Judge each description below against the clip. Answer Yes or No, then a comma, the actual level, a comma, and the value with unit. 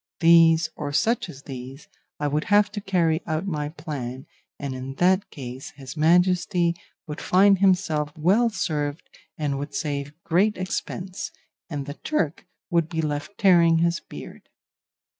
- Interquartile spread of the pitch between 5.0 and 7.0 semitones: No, average, 3.9 semitones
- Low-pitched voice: No, medium, 160 Hz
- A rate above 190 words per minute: No, average, 150 wpm